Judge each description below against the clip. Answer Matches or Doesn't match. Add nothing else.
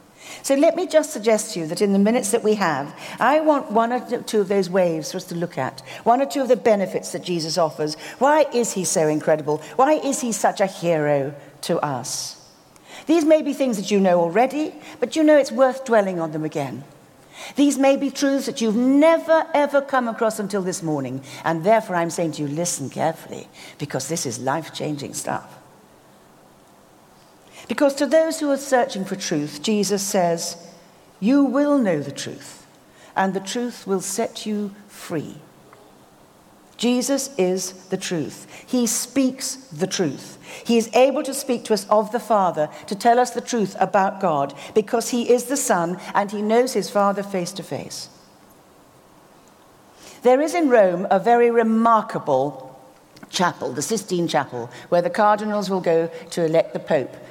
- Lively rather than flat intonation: Matches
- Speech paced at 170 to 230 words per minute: Matches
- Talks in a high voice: Matches